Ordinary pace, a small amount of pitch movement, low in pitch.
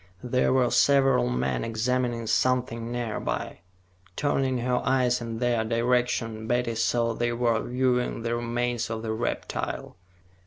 No: slow, 130 wpm; narrow, 1.5 semitones; low, 120 Hz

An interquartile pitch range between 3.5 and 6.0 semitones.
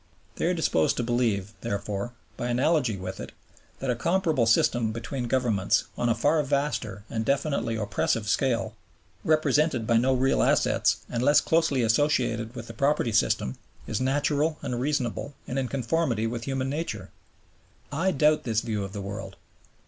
Yes: average, 4.3 semitones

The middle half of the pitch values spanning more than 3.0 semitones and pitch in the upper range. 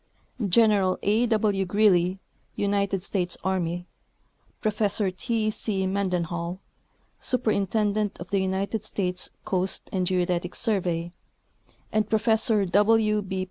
No: average, 2.7 semitones; high, 195 Hz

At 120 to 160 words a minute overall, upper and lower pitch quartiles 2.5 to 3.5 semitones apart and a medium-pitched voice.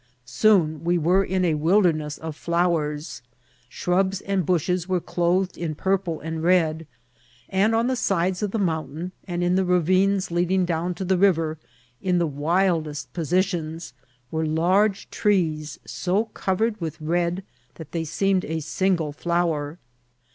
Yes: average, 155 wpm; average, 2.8 semitones; medium, 175 Hz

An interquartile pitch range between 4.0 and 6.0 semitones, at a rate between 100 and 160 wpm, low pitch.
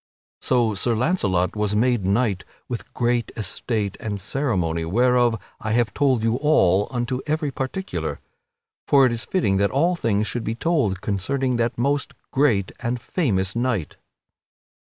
Yes: average, 4.4 semitones; average, 155 wpm; low, 120 Hz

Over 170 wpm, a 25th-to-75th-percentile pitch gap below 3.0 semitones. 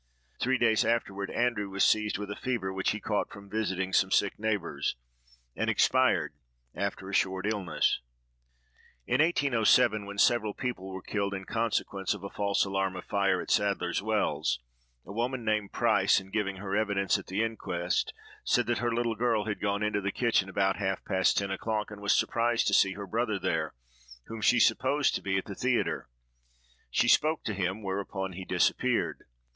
Yes: average, 185 wpm; narrow, 2.6 semitones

